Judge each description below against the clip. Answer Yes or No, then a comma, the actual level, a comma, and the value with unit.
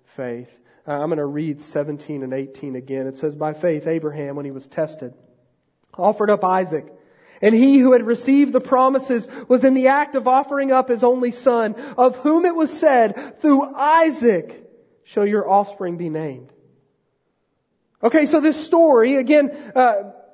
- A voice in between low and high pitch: No, high, 230 Hz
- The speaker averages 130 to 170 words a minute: Yes, average, 165 wpm